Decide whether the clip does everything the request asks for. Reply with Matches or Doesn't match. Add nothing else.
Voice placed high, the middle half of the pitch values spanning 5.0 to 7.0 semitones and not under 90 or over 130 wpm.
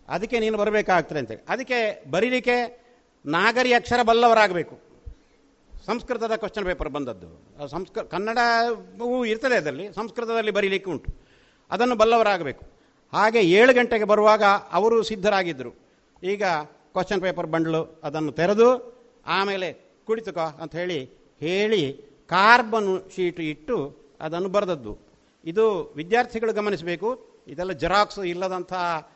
Matches